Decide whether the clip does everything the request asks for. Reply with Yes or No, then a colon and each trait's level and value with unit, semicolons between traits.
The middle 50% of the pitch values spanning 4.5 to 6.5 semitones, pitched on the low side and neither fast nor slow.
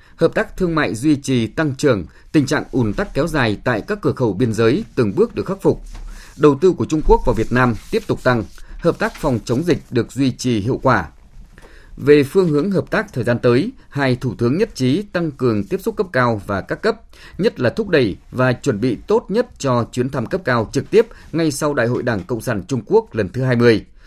Yes: average, 5.1 semitones; low, 130 Hz; average, 240 wpm